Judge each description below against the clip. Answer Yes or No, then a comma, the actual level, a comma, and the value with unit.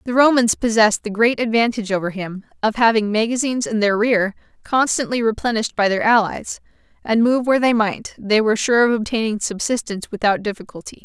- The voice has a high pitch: Yes, high, 220 Hz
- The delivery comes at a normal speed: Yes, average, 175 wpm